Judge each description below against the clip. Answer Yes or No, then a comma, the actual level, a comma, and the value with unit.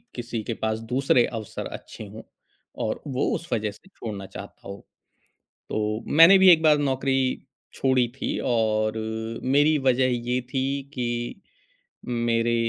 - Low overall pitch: Yes, low, 125 Hz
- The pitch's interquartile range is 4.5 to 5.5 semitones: No, average, 3.6 semitones